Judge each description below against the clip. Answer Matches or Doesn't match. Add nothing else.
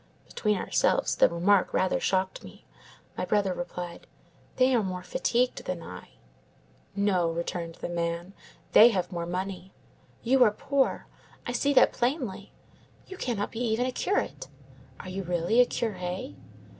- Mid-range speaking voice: Doesn't match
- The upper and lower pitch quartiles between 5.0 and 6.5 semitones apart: Matches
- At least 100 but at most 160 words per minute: Matches